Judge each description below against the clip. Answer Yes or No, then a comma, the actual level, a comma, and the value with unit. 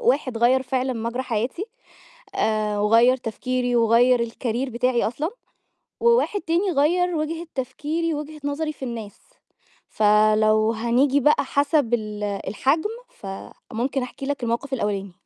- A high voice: Yes, very high, 250 Hz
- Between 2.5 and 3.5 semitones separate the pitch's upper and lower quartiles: No, average, 4.2 semitones